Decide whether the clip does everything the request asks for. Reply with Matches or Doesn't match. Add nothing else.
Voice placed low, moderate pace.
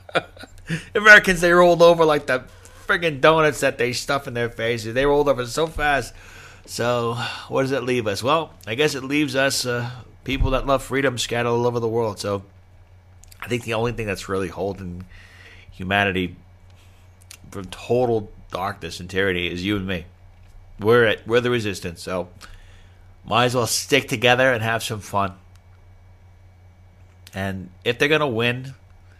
Matches